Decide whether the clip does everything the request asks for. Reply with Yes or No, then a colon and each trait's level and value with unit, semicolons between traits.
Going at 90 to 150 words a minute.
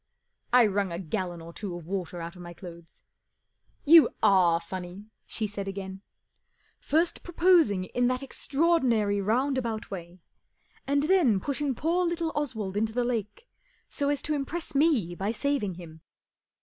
No: average, 165 wpm